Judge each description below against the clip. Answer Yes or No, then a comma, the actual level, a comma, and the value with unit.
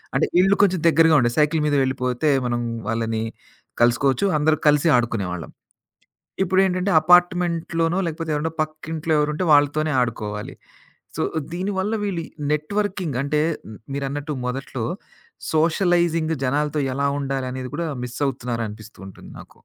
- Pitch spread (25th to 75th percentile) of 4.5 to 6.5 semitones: Yes, average, 4.8 semitones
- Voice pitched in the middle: Yes, medium, 150 Hz